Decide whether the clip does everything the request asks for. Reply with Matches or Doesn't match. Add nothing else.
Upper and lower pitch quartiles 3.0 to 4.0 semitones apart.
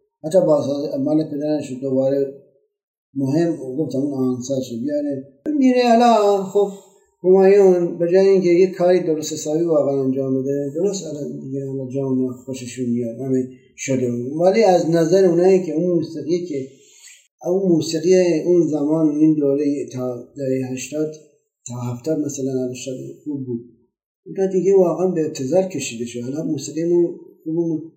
Doesn't match